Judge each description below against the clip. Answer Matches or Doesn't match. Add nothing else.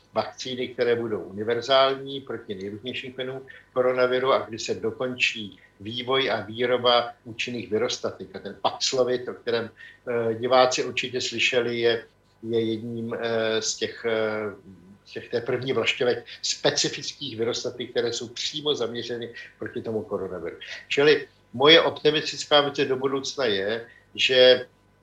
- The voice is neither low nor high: Doesn't match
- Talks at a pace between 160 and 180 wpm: Doesn't match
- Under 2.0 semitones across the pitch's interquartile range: Doesn't match